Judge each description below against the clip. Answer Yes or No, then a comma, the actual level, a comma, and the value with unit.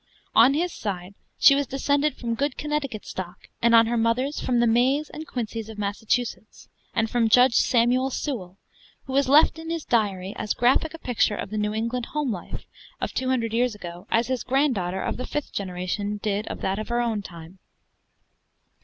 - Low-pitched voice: No, high, 235 Hz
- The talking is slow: No, average, 195 wpm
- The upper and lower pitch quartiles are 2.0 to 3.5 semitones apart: No, average, 4.2 semitones